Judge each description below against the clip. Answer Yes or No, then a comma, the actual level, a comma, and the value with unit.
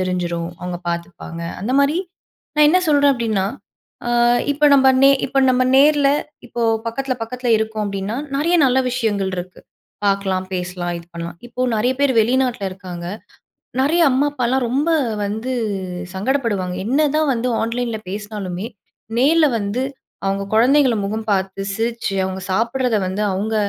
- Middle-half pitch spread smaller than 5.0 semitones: No, wide, 5.5 semitones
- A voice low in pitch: No, high, 225 Hz